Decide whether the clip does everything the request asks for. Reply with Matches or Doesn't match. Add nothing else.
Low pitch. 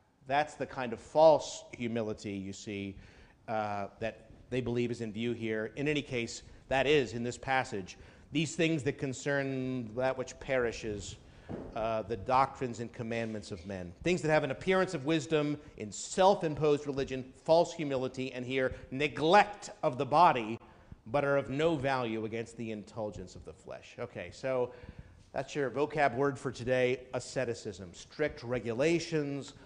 Matches